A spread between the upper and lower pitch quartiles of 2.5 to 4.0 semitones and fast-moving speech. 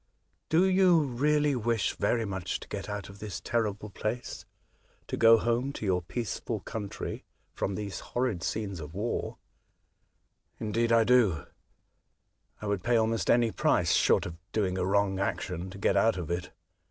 No: average, 3.7 semitones; average, 185 wpm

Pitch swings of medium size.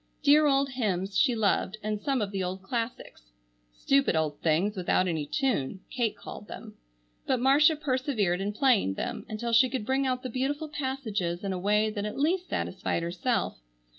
No: wide, 5.8 semitones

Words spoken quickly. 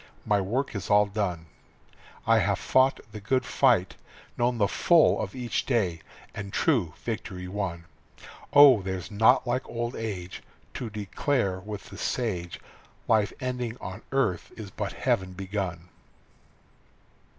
No: average, 140 wpm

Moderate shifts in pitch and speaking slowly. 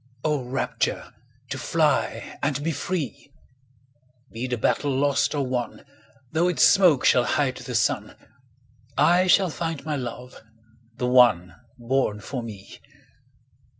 Yes: average, 3.8 semitones; slow, 130 wpm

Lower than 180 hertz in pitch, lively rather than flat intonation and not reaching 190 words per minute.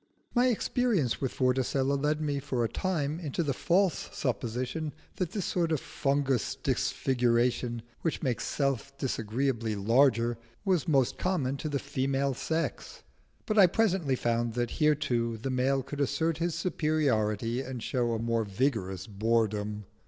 No: low, 135 Hz; average, 4.6 semitones; average, 150 wpm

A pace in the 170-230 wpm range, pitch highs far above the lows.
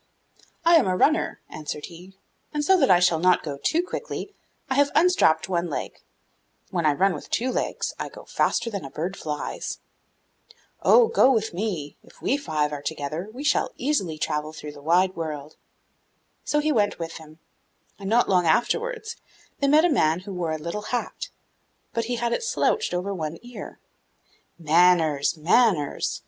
Yes: average, 180 wpm; wide, 8.0 semitones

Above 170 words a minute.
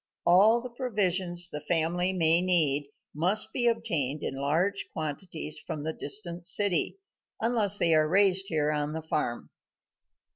No: average, 145 wpm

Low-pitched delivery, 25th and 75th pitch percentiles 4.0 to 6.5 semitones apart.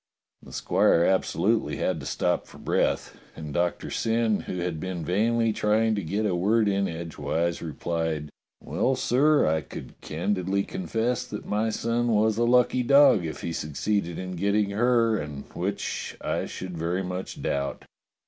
Yes: low, 100 Hz; average, 4.9 semitones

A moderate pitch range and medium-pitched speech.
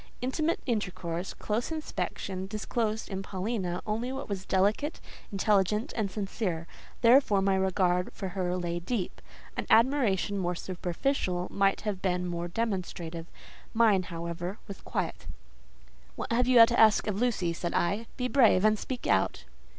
No: average, 4.1 semitones; high, 195 Hz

